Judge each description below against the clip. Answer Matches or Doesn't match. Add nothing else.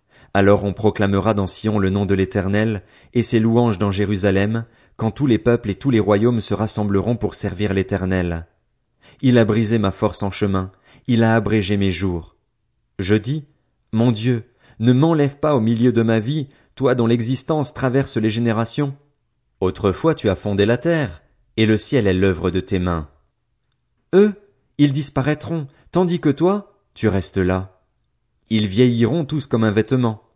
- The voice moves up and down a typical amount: Matches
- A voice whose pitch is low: Matches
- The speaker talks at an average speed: Matches